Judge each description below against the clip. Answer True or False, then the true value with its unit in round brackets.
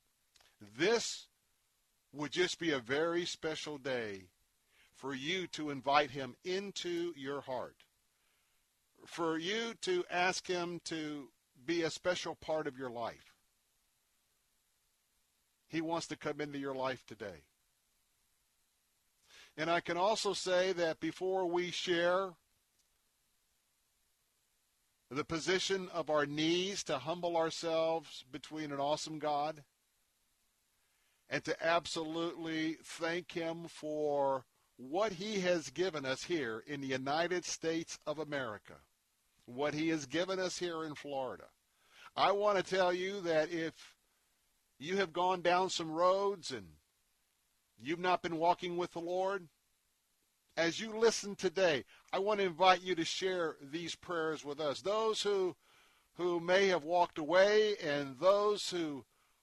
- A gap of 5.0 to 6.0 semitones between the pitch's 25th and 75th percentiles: False (3.4 semitones)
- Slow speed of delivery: True (130 wpm)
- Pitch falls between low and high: True (165 Hz)